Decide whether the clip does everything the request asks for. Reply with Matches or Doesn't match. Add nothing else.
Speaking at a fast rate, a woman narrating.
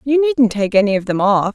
Matches